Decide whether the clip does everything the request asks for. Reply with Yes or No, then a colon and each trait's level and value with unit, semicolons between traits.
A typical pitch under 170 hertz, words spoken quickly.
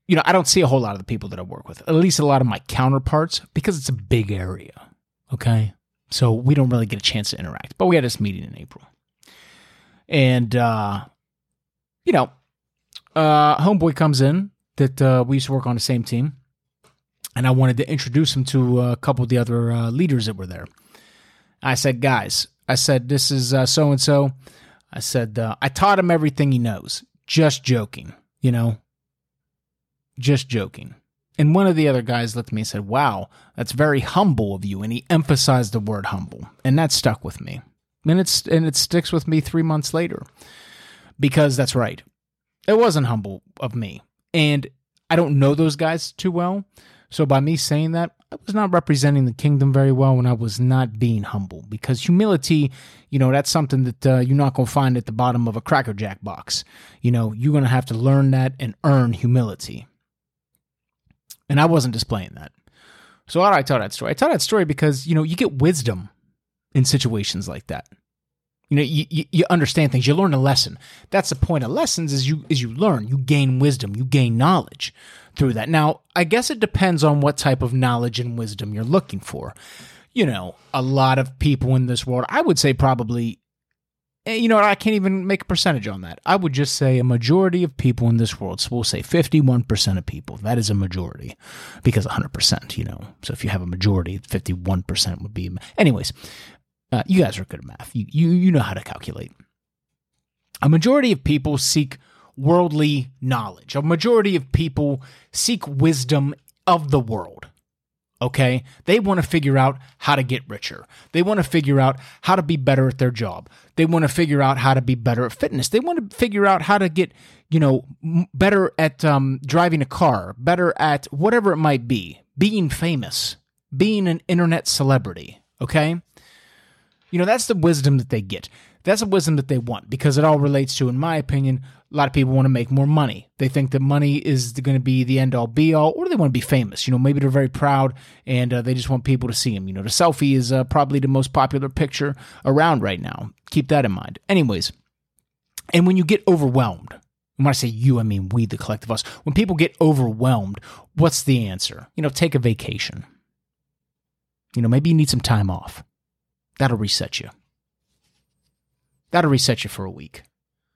Yes: low, 135 Hz; fast, 210 wpm